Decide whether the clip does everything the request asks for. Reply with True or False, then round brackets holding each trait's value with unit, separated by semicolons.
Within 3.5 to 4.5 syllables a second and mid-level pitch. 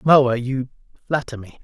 False (4.4 syllables/s; 130 Hz)